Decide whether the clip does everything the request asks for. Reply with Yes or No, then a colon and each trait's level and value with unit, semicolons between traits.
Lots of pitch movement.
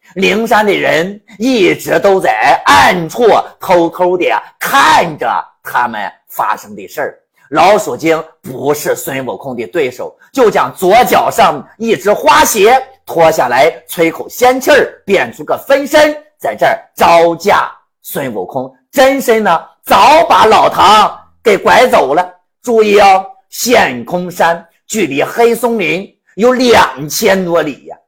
Yes: wide, 7.5 semitones